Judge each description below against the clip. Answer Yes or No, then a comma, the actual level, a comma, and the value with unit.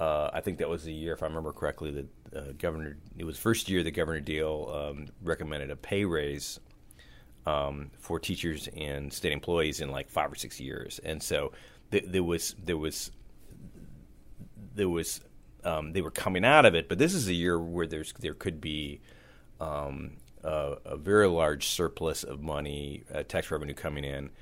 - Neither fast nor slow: Yes, average, 190 wpm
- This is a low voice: Yes, very low, 75 Hz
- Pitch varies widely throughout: No, average, 2.7 semitones